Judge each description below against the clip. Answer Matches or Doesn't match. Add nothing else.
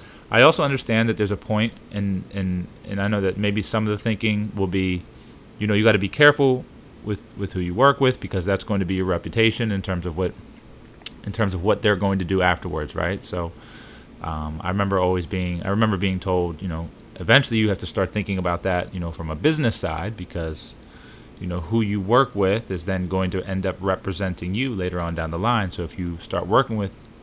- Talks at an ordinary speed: Doesn't match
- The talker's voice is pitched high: Doesn't match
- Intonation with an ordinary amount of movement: Matches